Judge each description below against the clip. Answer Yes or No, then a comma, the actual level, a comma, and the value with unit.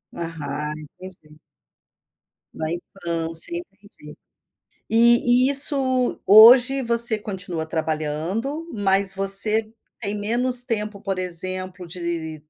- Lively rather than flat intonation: Yes, wide, 5.9 semitones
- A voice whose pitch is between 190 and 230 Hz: Yes, high, 195 Hz